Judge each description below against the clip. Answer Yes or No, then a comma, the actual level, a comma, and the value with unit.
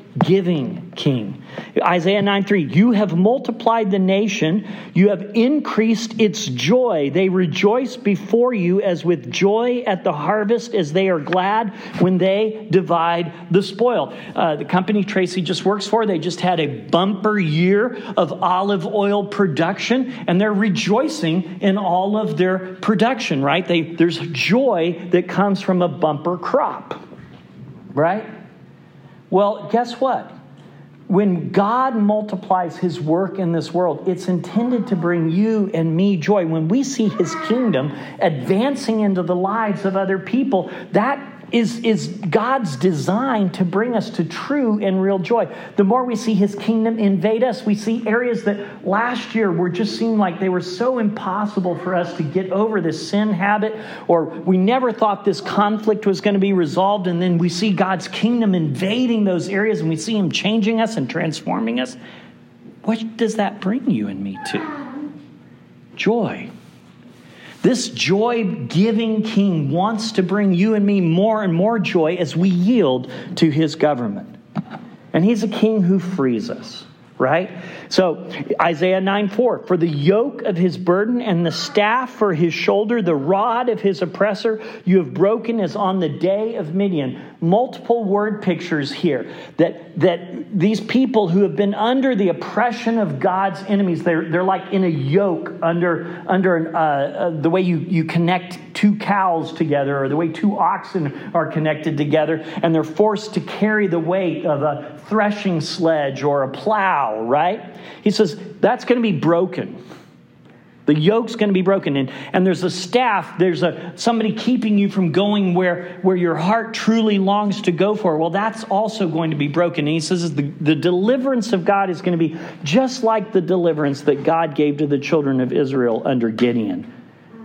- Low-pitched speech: No, high, 190 Hz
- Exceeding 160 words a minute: Yes, average, 170 wpm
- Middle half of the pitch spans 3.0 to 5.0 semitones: Yes, average, 3.8 semitones